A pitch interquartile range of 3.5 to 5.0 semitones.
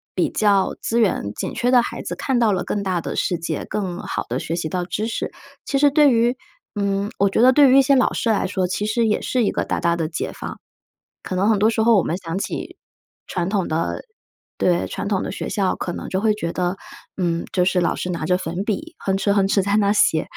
Yes: average, 3.9 semitones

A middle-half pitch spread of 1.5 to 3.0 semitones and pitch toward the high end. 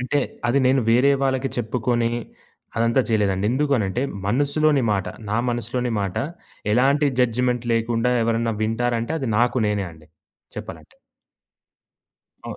No: narrow, 2.6 semitones; low, 120 Hz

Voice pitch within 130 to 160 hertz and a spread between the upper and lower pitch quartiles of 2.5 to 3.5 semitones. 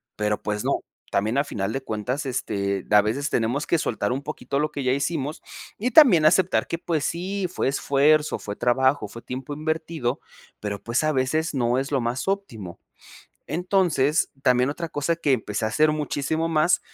No: medium, 140 Hz; average, 4.7 semitones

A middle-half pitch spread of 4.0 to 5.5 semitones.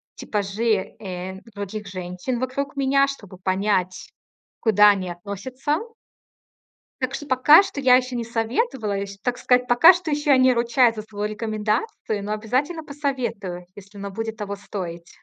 Yes: average, 4.5 semitones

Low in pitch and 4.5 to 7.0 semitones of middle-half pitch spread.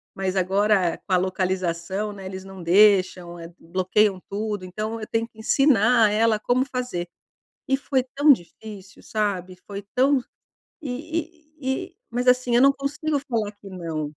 No: high, 210 Hz; average, 5.2 semitones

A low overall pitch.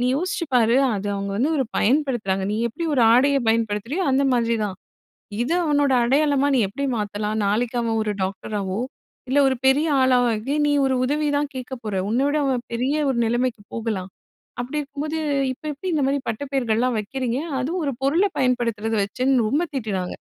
No: very high, 250 Hz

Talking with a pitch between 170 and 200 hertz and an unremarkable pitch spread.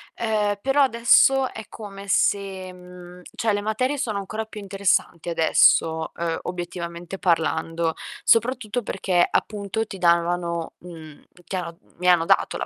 Yes: high, 190 Hz; average, 4.0 semitones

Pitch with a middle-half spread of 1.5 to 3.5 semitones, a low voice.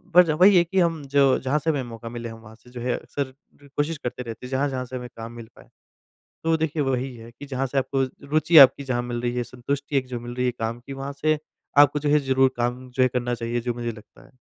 Yes: average, 2.9 semitones; low, 130 Hz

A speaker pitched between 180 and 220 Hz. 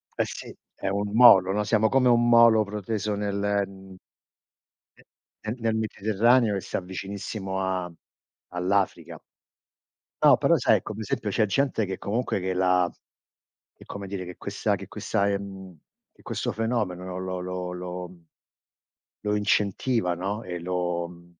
No: low, 100 Hz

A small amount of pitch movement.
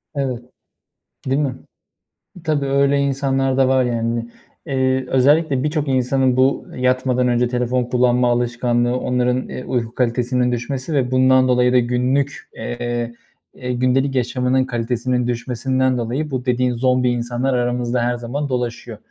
Yes: narrow, 1.4 semitones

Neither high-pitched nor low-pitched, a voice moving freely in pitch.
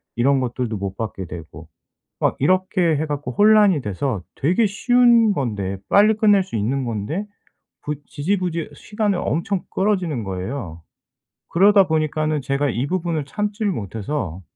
Yes: medium, 150 Hz; wide, 9.0 semitones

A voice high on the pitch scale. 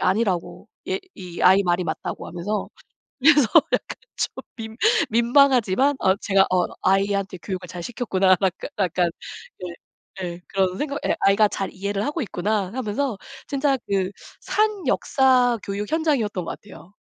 Yes: high, 200 Hz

